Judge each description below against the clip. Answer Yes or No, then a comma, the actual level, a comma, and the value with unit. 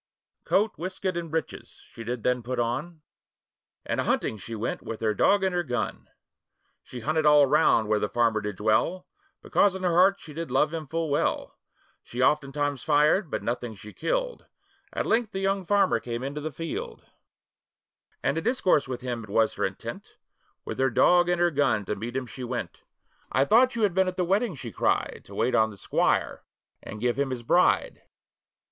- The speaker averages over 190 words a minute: Yes, average, 200 wpm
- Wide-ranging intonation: Yes, wide, 7.0 semitones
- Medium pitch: Yes, medium, 145 Hz